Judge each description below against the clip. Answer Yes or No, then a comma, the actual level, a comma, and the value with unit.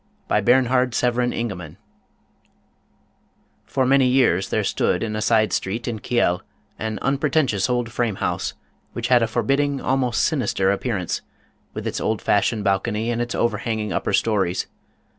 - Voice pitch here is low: Yes, low, 115 Hz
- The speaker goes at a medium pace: Yes, average, 165 wpm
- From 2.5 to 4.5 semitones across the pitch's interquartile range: Yes, average, 3.1 semitones